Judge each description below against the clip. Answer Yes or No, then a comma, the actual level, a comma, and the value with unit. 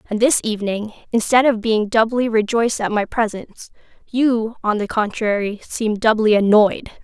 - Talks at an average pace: Yes, average, 155 wpm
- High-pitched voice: Yes, high, 220 Hz